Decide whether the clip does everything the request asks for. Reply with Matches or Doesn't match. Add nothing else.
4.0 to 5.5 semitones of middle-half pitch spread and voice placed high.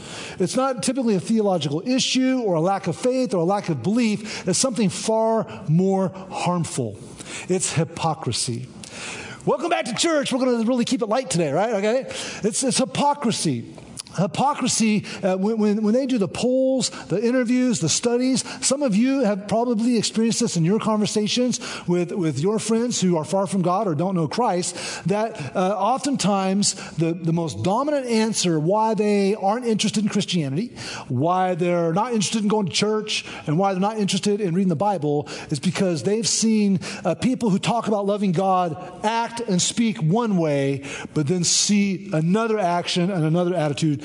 Matches